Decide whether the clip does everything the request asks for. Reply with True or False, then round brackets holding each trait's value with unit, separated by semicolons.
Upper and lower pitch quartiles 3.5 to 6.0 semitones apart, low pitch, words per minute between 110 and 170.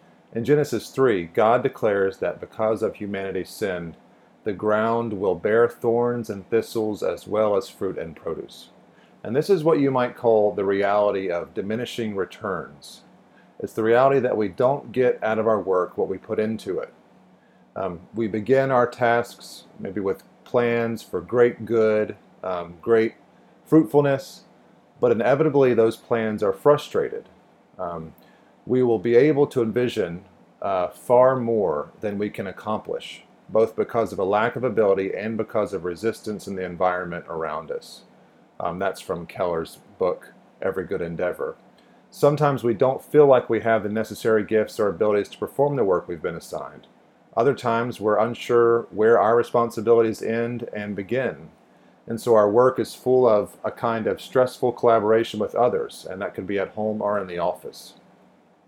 False (2.7 semitones; 115 Hz; 165 wpm)